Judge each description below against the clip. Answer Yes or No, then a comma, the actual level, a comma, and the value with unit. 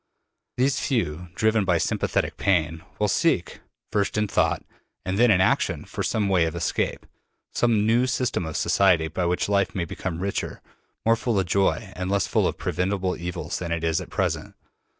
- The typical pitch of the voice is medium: No, very low, 95 Hz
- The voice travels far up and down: No, average, 3.5 semitones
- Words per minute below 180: No, average, 185 wpm